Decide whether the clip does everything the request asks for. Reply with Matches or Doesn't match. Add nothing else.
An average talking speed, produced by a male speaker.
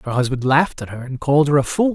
Doesn't match